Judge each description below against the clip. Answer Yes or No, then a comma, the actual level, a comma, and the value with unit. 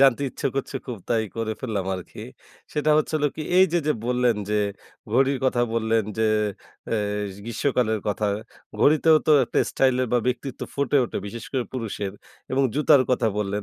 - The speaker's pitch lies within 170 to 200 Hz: No, low, 125 Hz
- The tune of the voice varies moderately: Yes, average, 3.7 semitones